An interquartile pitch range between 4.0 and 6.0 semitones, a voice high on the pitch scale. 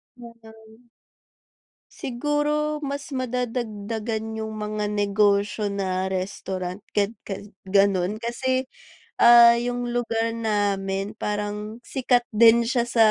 No: average, 2.8 semitones; high, 220 Hz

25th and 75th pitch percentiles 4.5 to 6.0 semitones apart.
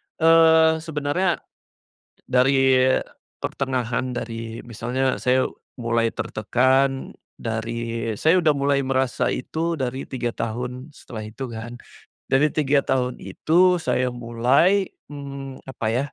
No: average, 3.4 semitones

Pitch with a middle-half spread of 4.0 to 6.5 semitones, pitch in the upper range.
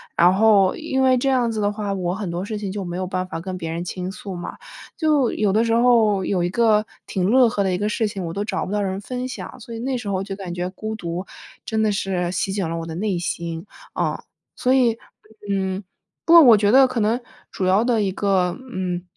No: average, 3.6 semitones; high, 200 Hz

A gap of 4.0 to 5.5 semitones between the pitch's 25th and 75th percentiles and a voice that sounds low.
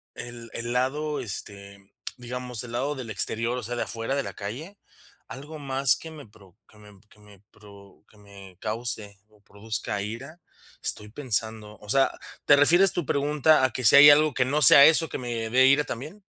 Yes: average, 5.1 semitones; low, 120 Hz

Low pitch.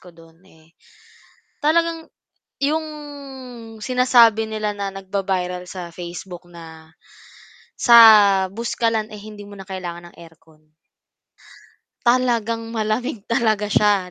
No: high, 205 Hz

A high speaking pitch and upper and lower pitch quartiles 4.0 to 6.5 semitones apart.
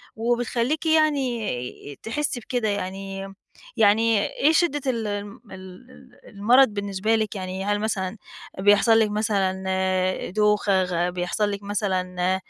No: high, 205 Hz; average, 3.3 semitones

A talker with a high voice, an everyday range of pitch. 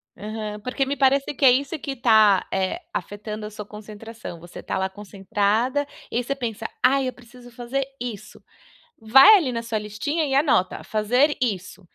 Yes: high, 230 Hz; average, 4.2 semitones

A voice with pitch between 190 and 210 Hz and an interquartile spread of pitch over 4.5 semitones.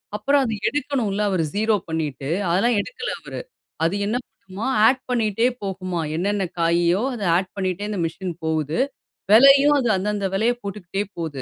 Yes: high, 200 Hz; average, 5.2 semitones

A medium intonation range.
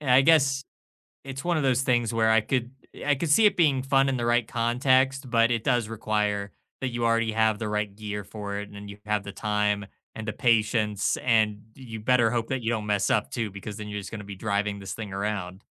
Yes: average, 3.4 semitones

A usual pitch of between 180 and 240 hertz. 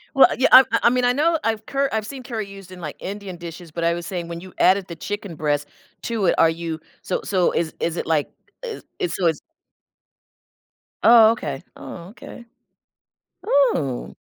Yes: medium, 185 Hz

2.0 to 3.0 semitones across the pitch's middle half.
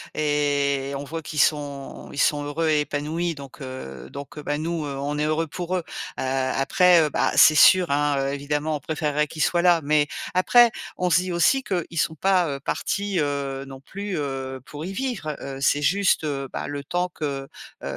No: average, 3.4 semitones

